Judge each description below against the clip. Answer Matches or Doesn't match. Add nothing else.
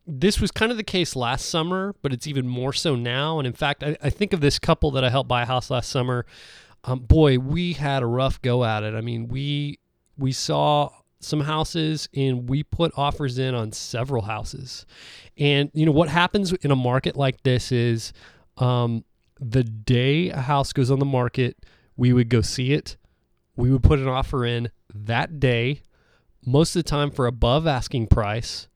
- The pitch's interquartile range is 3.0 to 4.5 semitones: Matches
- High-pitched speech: Doesn't match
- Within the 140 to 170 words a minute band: Doesn't match